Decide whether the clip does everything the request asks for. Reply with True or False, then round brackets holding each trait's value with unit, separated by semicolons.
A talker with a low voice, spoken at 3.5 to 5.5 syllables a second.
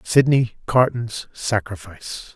True (110 Hz; 3.8 syllables/s)